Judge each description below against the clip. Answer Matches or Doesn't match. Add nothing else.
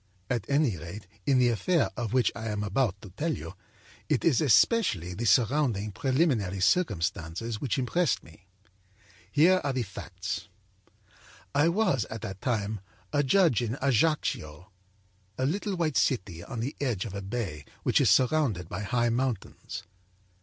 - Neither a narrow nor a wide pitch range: Doesn't match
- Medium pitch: Doesn't match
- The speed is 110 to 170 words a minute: Matches